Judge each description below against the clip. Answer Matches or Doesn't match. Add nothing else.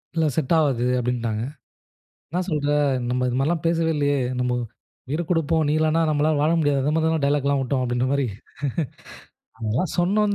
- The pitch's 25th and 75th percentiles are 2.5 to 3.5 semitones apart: Doesn't match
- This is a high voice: Doesn't match